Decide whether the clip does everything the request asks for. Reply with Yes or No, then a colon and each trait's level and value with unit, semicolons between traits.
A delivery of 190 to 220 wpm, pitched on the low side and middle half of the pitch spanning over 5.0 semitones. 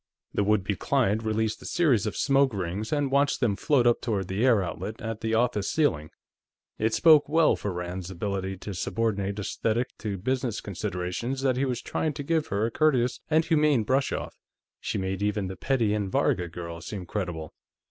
Yes: average, 195 wpm; low, 110 Hz; wide, 5.5 semitones